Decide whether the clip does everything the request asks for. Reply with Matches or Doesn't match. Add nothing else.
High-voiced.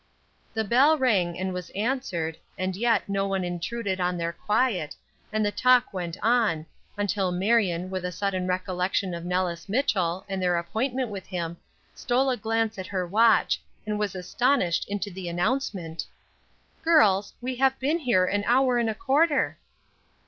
Matches